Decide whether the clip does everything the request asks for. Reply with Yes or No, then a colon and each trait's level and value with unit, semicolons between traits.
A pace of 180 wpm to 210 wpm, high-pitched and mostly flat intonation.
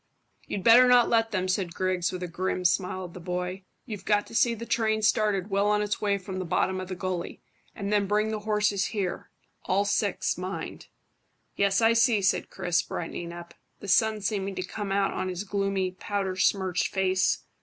Yes: average, 200 wpm; high, 195 Hz; narrow, 2.2 semitones